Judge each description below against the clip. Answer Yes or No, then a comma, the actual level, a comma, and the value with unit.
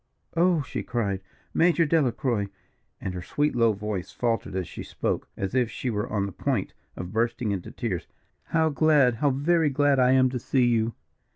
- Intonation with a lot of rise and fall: Yes, wide, 5.7 semitones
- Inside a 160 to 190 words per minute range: Yes, average, 185 wpm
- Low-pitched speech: Yes, low, 120 Hz